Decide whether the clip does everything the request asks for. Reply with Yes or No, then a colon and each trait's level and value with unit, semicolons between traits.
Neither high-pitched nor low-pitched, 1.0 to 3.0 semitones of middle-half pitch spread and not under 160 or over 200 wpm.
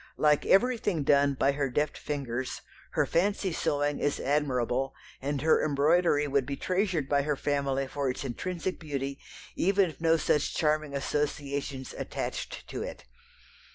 No: medium, 145 Hz; narrow, 2.5 semitones; average, 150 wpm